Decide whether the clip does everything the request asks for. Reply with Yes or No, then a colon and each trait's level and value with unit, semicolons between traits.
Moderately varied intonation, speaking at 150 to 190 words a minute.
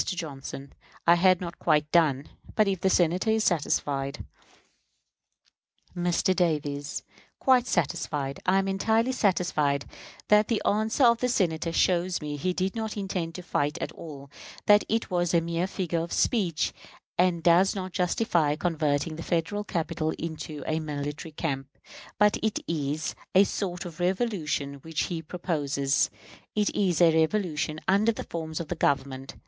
Yes: average, 4.0 semitones; average, 155 wpm